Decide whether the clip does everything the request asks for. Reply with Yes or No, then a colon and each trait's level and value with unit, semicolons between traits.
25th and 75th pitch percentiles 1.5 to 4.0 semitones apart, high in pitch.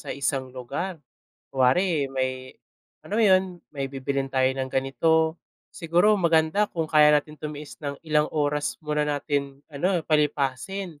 No: average, 3.2 semitones; medium, 150 Hz